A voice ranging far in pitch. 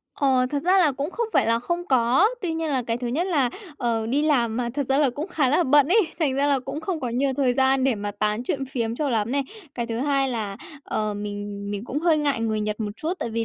No: average, 4.3 semitones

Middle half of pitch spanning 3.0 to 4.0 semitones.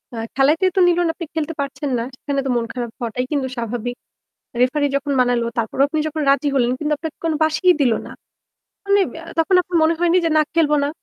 No: average, 4.6 semitones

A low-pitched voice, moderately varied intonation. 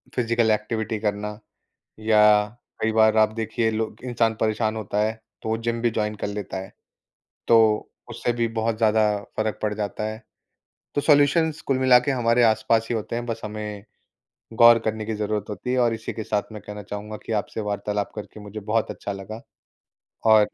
No: low, 110 Hz; narrow, 1.5 semitones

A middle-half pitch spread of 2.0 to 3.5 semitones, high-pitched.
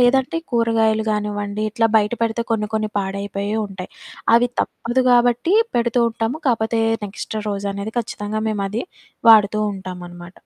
Yes: narrow, 2.4 semitones; high, 215 Hz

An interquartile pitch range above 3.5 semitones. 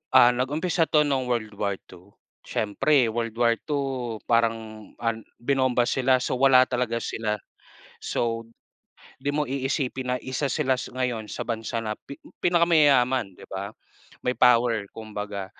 No: average, 3.0 semitones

